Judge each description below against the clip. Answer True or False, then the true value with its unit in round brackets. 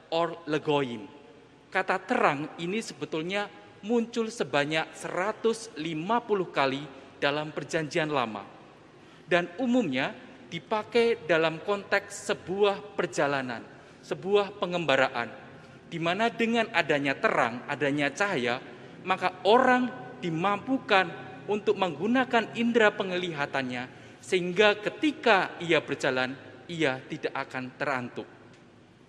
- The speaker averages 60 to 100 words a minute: True (90 wpm)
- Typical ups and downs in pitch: False (6.3 semitones)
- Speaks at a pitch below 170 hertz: False (175 Hz)